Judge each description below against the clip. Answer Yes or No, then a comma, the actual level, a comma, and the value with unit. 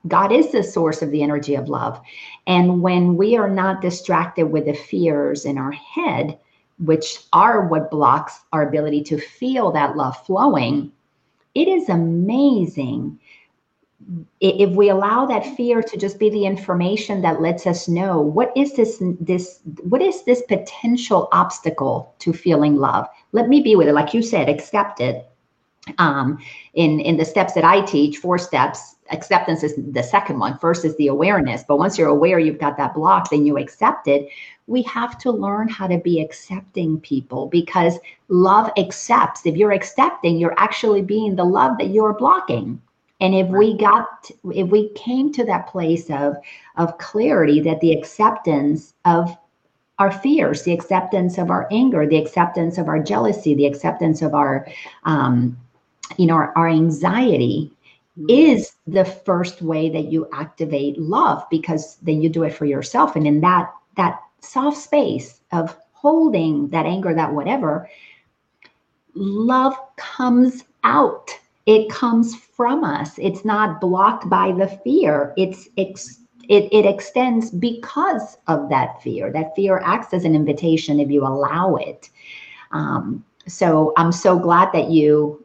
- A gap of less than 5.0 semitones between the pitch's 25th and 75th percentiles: No, average, 5.3 semitones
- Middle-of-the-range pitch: Yes, medium, 175 Hz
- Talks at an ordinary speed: Yes, average, 160 wpm